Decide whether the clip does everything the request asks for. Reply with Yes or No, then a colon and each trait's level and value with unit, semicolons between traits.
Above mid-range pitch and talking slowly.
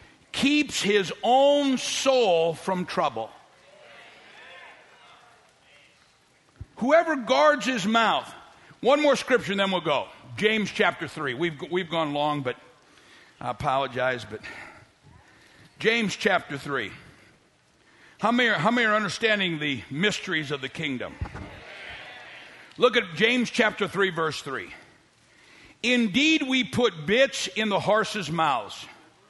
Yes: high, 205 Hz; slow, 120 wpm